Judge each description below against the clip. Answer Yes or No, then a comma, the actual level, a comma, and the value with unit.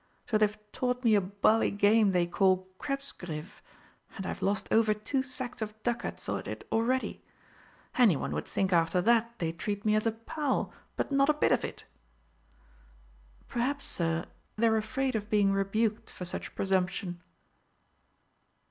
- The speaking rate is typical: Yes, average, 155 wpm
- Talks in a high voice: Yes, high, 215 Hz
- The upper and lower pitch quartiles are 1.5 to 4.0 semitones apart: Yes, average, 3.7 semitones